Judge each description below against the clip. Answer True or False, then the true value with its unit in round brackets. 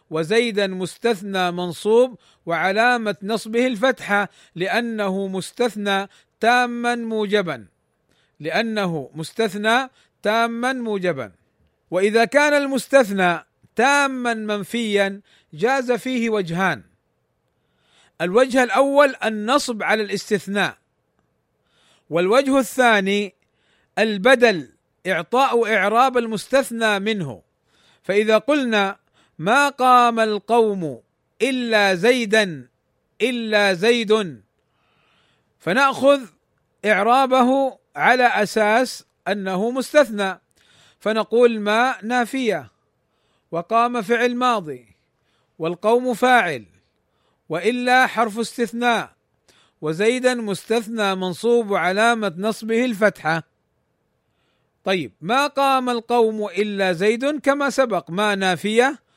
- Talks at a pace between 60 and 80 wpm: True (75 wpm)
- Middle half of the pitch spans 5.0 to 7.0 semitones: False (4.0 semitones)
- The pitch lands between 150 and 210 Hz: False (220 Hz)